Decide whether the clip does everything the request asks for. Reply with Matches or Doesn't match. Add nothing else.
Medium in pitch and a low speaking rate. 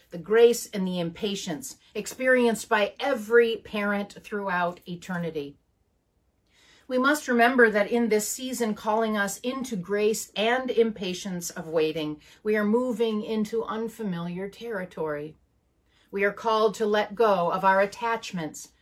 Doesn't match